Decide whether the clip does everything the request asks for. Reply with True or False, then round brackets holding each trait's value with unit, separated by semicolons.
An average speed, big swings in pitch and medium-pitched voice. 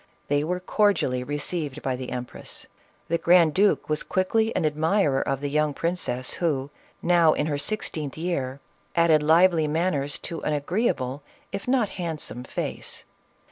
False (150 wpm; 3.9 semitones; 155 Hz)